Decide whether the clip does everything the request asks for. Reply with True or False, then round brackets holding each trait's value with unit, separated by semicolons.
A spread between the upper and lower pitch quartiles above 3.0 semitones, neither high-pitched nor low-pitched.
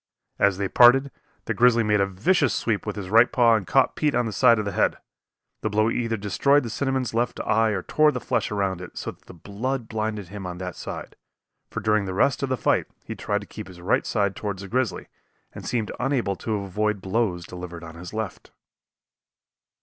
False (3.6 semitones; 105 Hz)